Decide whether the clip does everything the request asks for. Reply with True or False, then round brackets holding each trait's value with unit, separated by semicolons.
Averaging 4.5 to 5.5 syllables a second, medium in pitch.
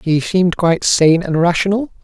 True (5.2 syllables/s; 175 Hz)